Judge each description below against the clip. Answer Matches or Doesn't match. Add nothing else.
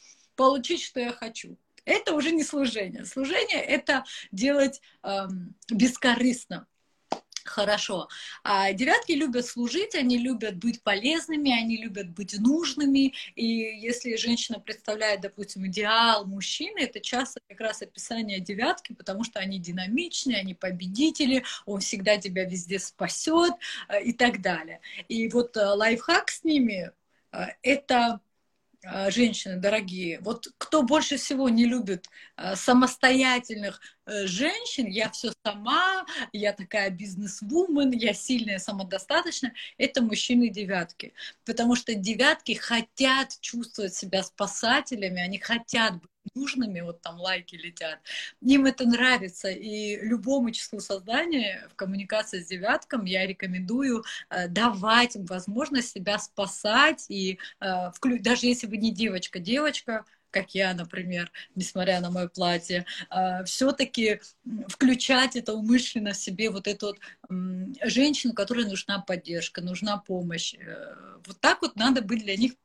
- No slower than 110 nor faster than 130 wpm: Matches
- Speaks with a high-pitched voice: Matches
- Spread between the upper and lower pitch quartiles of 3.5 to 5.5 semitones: Matches